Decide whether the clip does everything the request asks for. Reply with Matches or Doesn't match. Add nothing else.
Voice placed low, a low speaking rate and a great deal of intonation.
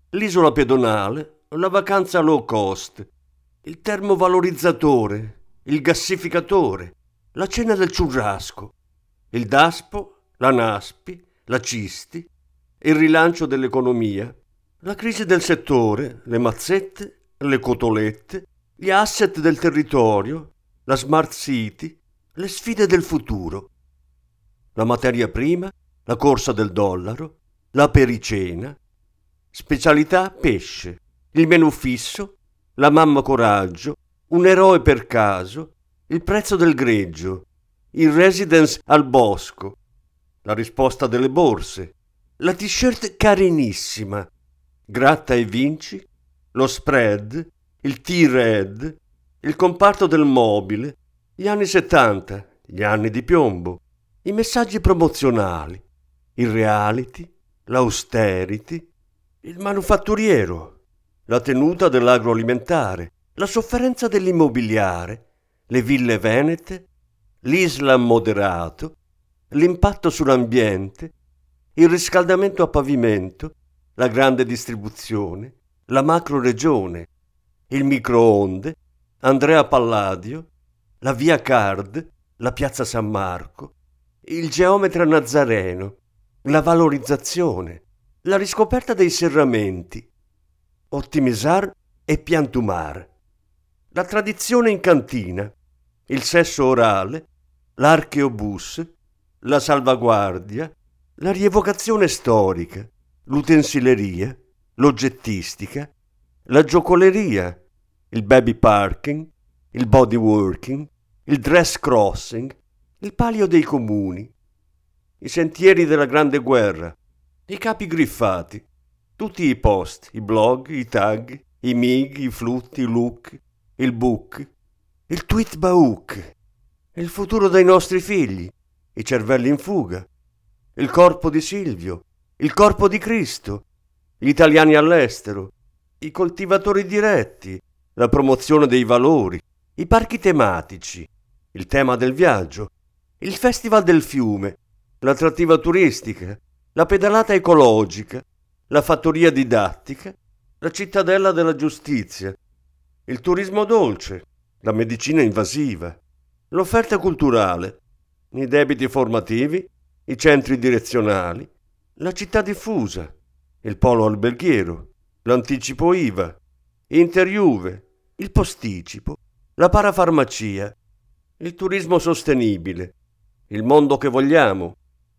Matches